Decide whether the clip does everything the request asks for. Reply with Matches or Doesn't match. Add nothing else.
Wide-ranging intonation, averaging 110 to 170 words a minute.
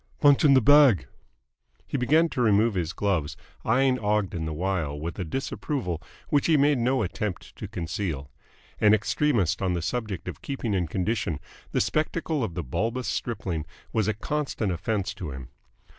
Matches